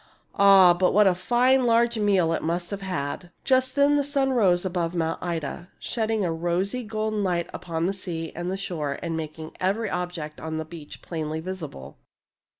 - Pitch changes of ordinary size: Yes, average, 4.4 semitones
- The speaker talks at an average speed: Yes, average, 185 wpm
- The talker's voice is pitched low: No, medium, 180 Hz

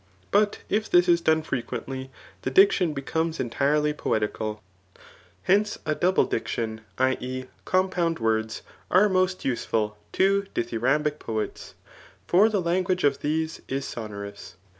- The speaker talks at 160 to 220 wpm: No, slow, 135 wpm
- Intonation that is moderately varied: No, wide, 7.5 semitones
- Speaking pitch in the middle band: Yes, medium, 150 Hz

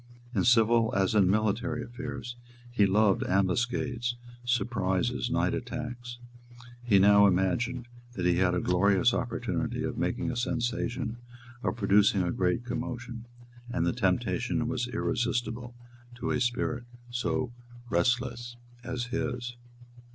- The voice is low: Yes, low, 120 Hz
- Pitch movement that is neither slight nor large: Yes, average, 3.4 semitones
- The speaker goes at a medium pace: No, slow, 125 wpm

